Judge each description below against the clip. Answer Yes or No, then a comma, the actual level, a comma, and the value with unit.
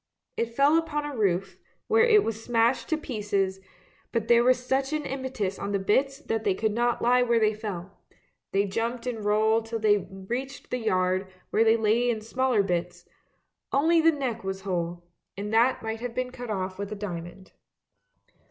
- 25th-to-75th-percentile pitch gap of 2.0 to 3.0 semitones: No, average, 4.2 semitones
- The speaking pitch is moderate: No, high, 225 Hz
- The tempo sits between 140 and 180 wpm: No, average, 190 wpm